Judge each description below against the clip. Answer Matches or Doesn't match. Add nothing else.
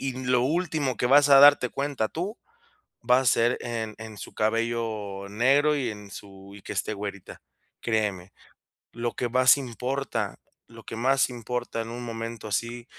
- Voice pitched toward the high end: Doesn't match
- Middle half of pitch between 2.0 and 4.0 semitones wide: Matches